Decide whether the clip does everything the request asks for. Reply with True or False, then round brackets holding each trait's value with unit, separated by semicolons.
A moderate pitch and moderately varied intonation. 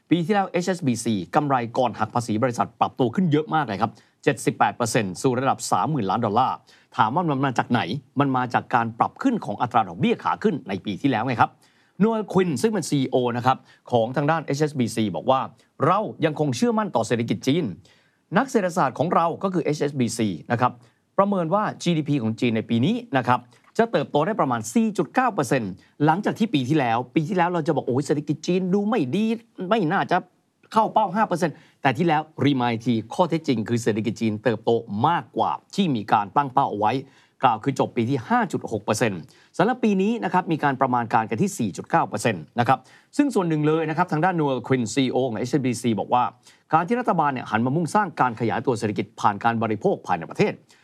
False (145 Hz; 6.8 semitones)